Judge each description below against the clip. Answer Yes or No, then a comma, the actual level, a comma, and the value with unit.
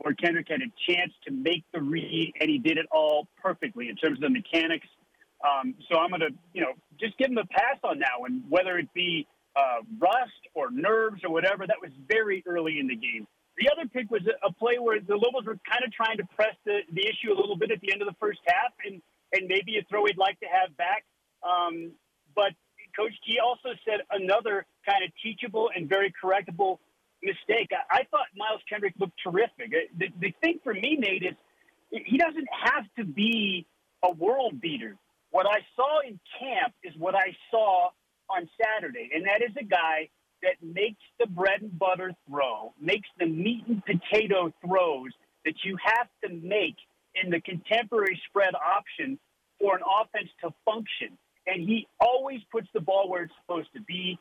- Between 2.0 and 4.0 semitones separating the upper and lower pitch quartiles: No, average, 4.8 semitones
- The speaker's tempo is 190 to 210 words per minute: Yes, average, 200 wpm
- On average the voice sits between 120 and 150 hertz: No, high, 200 Hz